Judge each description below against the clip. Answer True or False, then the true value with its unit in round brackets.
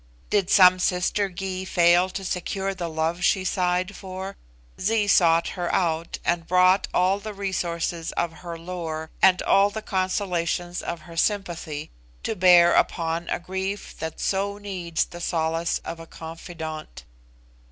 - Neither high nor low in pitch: True (180 Hz)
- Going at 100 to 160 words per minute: True (150 wpm)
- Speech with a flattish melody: True (2.3 semitones)